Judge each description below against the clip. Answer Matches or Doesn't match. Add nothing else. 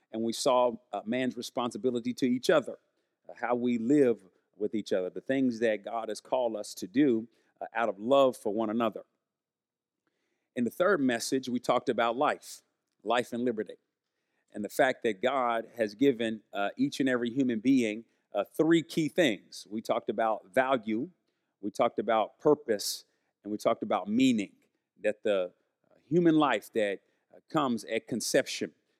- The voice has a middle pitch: Doesn't match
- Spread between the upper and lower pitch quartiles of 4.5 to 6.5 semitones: Doesn't match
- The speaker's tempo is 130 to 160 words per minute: Doesn't match